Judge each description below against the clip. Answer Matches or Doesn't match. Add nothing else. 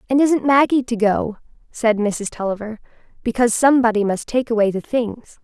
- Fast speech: Doesn't match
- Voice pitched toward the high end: Matches